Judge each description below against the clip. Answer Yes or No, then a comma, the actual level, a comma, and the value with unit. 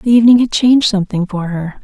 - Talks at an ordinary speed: No, fast, 230 wpm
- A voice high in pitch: Yes, high, 210 Hz